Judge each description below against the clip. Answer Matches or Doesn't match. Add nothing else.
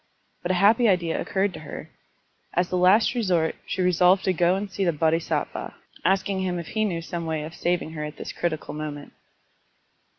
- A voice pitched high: Doesn't match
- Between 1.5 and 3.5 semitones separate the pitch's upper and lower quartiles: Matches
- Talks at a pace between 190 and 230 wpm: Matches